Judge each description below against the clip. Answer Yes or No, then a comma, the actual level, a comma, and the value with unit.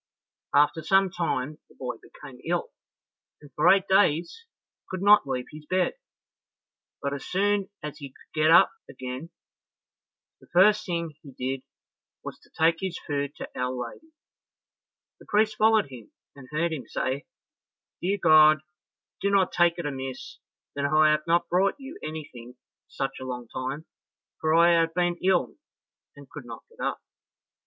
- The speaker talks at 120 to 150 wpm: No, average, 165 wpm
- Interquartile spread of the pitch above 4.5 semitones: Yes, average, 5.0 semitones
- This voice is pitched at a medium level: Yes, medium, 155 Hz